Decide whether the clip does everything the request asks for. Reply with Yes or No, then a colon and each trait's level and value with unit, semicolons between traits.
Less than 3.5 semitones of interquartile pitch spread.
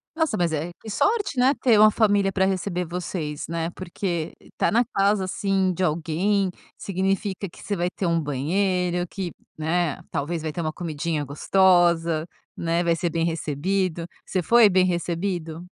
Yes: average, 2.9 semitones